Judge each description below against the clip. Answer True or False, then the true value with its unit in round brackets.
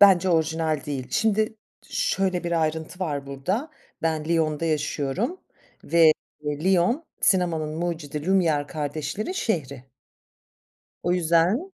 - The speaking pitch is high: False (165 Hz)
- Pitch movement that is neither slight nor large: True (3.8 semitones)